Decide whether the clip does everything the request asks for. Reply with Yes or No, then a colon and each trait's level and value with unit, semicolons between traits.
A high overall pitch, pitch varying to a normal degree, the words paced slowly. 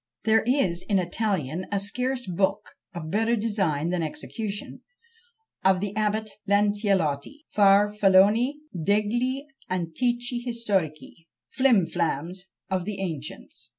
Yes: high, 200 Hz; average, 4.0 semitones; slow, 115 wpm